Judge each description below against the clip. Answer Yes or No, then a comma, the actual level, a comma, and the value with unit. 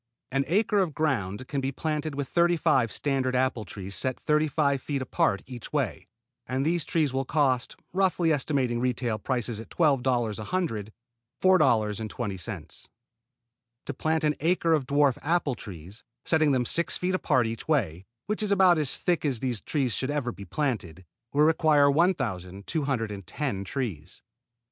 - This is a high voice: No, low, 135 Hz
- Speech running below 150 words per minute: No, average, 160 wpm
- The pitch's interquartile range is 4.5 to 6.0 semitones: Yes, wide, 5.4 semitones